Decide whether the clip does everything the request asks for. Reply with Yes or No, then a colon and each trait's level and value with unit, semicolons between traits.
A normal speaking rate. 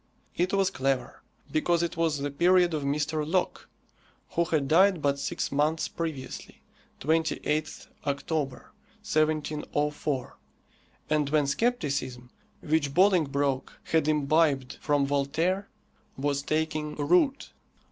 No: slow, 110 wpm